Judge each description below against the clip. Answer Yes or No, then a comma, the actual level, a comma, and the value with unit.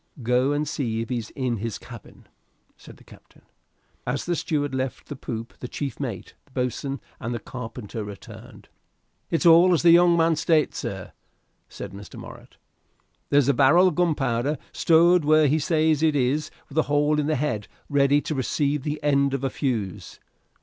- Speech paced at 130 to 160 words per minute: No, average, 175 wpm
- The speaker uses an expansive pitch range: No, average, 3.8 semitones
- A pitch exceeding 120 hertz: Yes, medium, 140 Hz